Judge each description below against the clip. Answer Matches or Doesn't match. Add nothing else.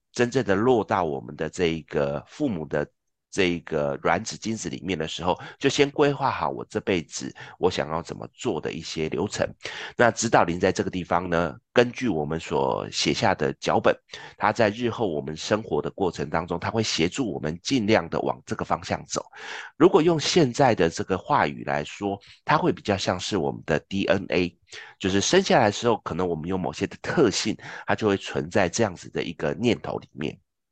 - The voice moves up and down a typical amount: Doesn't match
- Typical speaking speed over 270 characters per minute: Matches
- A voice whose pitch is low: Matches